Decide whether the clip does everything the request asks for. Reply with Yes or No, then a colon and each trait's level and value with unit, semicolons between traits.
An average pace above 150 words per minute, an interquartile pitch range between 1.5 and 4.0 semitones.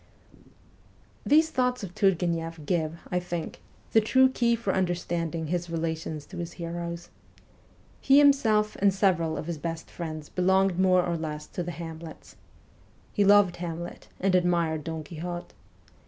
No: average, 145 wpm; average, 2.8 semitones